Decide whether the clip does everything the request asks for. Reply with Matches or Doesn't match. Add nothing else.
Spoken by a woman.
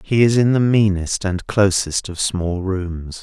Doesn't match